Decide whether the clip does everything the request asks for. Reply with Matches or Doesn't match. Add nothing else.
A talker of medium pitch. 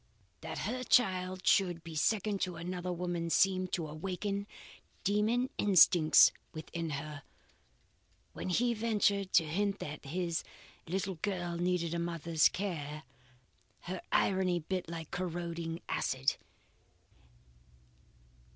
Matches